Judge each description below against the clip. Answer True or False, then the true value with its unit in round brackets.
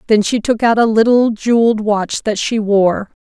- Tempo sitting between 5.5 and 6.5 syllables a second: False (4.7 syllables/s)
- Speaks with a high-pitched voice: True (220 Hz)